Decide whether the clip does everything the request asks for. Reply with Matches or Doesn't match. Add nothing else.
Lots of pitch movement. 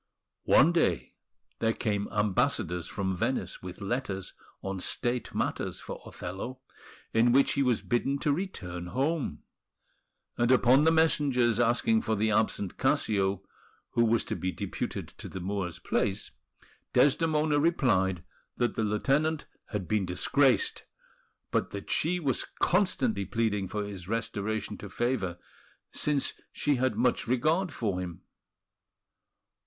Matches